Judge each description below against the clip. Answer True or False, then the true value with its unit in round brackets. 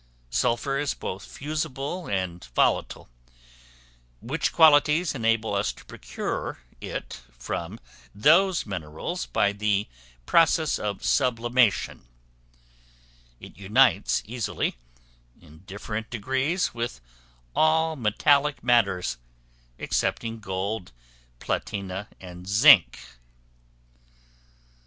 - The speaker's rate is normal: False (85 wpm)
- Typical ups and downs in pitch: False (6.4 semitones)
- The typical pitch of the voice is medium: False (115 Hz)